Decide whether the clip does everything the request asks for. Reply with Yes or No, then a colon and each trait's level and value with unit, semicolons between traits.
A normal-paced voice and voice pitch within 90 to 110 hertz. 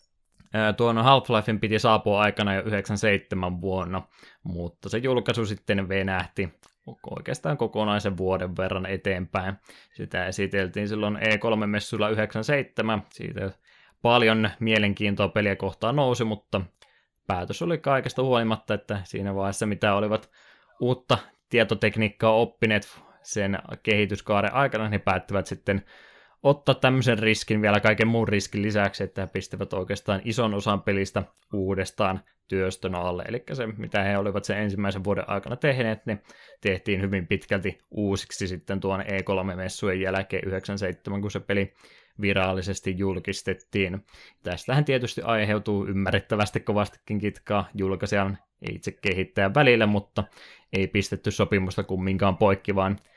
Yes: average, 125 wpm; low, 100 Hz